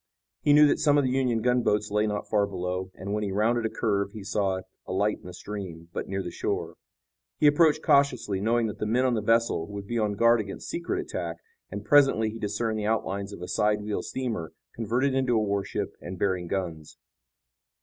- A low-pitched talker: Yes, low, 105 Hz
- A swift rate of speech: Yes, fast, 210 wpm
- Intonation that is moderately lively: Yes, average, 3.3 semitones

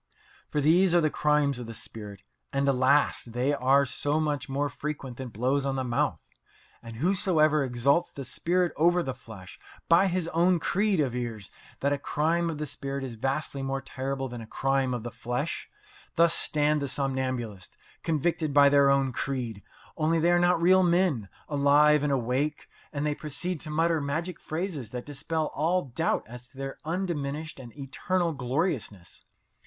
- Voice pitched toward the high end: No, medium, 140 Hz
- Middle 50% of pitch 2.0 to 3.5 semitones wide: No, average, 3.9 semitones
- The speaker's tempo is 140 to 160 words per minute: No, average, 175 wpm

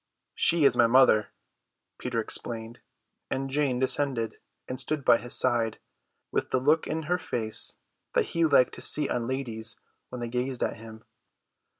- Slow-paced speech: No, average, 165 wpm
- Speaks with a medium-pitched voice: No, low, 125 Hz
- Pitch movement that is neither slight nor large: Yes, average, 3.0 semitones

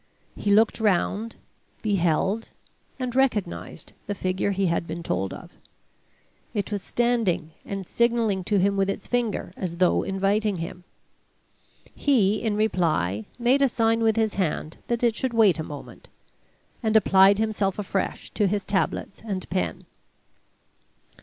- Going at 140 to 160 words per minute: Yes, average, 145 wpm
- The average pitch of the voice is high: Yes, high, 200 Hz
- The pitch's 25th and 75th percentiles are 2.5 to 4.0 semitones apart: Yes, average, 3.3 semitones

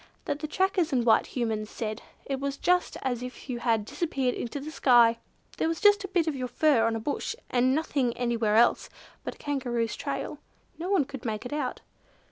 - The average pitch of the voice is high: Yes, very high, 255 Hz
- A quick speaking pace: Yes, fast, 210 wpm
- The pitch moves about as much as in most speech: Yes, average, 4.6 semitones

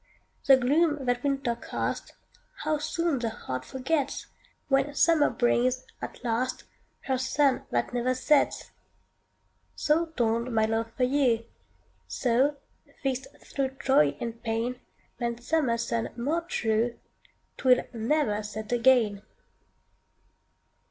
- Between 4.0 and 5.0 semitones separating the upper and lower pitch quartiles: No, average, 3.2 semitones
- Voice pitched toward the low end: No, very high, 250 Hz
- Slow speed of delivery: Yes, slow, 120 wpm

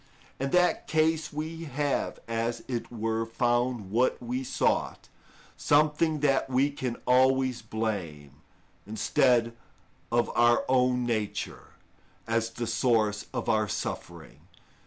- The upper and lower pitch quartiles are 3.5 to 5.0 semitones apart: No, average, 3.1 semitones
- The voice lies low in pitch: Yes, low, 120 Hz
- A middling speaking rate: No, slow, 115 wpm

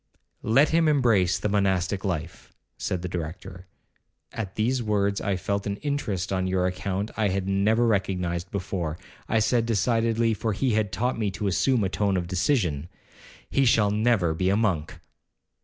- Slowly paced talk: No, average, 170 wpm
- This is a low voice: Yes, low, 100 Hz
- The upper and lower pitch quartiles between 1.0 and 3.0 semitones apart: No, average, 3.5 semitones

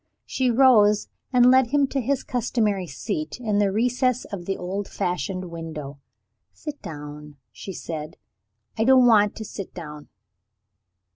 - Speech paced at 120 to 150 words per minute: Yes, average, 145 wpm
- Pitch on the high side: Yes, high, 205 Hz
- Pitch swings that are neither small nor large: No, wide, 6.8 semitones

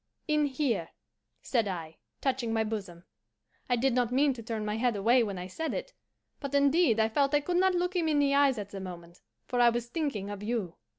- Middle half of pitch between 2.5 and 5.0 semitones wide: No, wide, 5.4 semitones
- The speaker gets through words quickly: Yes, fast, 225 wpm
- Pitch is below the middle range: No, high, 240 Hz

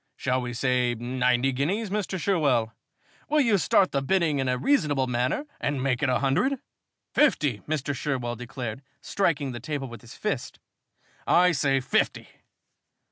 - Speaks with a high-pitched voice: No, low, 135 Hz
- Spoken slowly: No, average, 155 wpm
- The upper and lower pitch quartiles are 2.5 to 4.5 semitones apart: No, average, 4.9 semitones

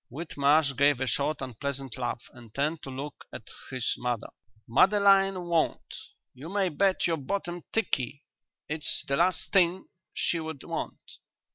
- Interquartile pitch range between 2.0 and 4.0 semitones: No, average, 4.6 semitones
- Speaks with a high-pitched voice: No, medium, 150 Hz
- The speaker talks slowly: No, average, 145 wpm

